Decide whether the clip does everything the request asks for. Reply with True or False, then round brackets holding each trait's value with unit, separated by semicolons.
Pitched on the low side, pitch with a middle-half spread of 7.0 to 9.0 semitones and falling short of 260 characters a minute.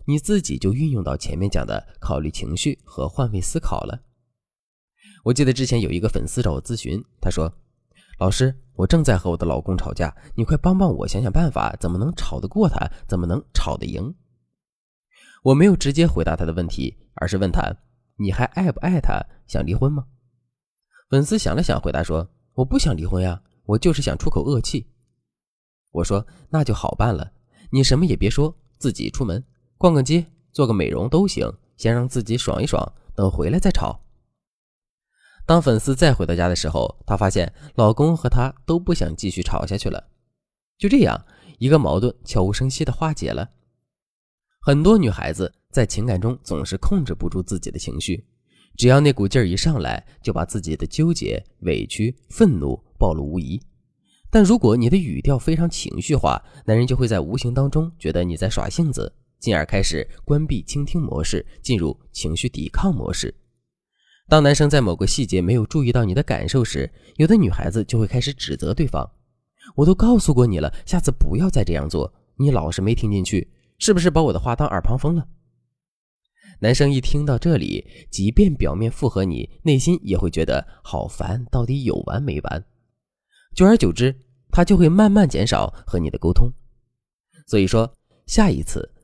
False (120 Hz; 7.3 semitones; 270 characters per minute)